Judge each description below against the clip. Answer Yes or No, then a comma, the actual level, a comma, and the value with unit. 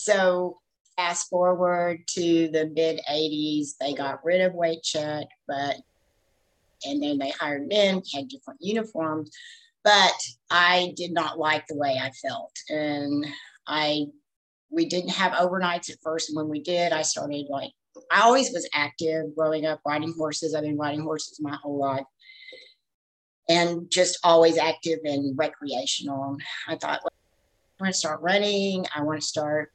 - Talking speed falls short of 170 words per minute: Yes, average, 160 wpm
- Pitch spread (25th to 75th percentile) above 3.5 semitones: No, average, 3.2 semitones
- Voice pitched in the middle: Yes, medium, 155 Hz